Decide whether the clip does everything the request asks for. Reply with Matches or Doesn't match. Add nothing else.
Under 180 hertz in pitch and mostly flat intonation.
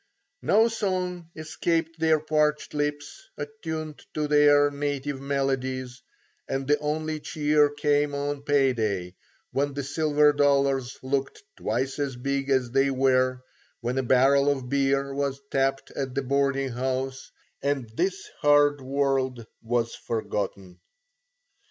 Matches